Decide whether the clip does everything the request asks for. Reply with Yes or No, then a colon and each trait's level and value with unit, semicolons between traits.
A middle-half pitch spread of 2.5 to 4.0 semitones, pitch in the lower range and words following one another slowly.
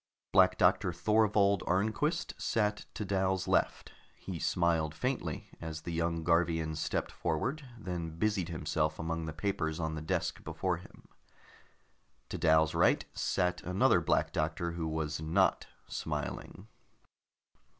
Yes: average, 3.7 semitones; very low, 85 Hz; slow, 130 wpm